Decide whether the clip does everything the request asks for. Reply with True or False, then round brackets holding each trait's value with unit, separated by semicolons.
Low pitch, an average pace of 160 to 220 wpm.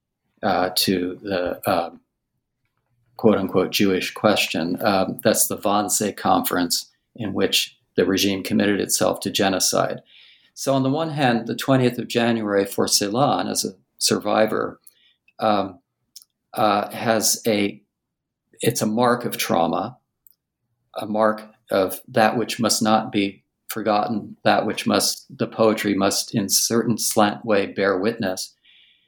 False (110 Hz; 135 wpm)